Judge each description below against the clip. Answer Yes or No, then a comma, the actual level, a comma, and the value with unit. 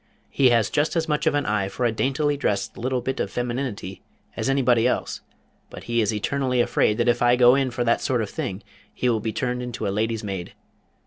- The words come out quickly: Yes, fast, 230 wpm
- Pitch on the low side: Yes, low, 120 Hz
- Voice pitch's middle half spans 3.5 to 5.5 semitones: No, average, 3.0 semitones